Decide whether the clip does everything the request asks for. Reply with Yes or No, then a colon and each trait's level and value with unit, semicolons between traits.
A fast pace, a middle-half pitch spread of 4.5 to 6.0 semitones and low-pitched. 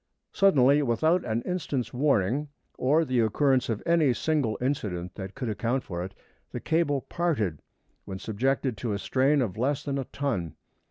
No: average, 165 wpm; average, 5.0 semitones; low, 130 Hz